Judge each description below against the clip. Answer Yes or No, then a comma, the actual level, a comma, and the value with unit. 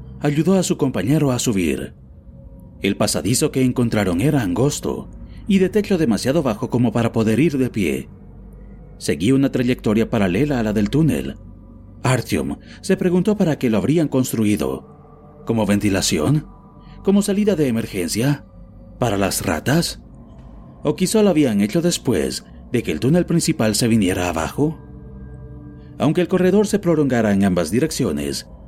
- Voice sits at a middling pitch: No, low, 120 Hz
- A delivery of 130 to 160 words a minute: Yes, average, 145 wpm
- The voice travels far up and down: Yes, wide, 7.7 semitones